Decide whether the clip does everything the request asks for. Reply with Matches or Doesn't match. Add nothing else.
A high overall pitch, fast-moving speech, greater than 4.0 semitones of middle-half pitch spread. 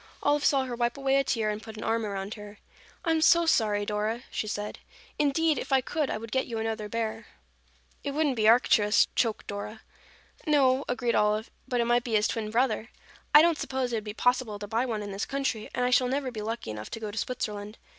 Doesn't match